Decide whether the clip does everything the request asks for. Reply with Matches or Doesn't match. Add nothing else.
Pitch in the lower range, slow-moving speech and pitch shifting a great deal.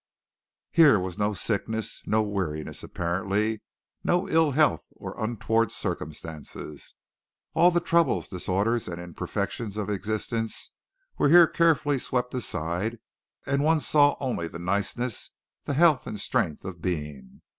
Matches